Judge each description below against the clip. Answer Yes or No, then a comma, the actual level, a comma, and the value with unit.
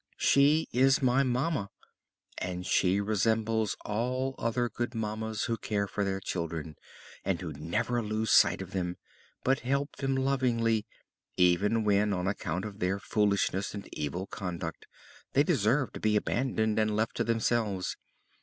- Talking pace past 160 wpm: No, average, 150 wpm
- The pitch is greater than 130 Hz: No, low, 110 Hz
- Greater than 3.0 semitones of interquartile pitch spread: Yes, average, 3.8 semitones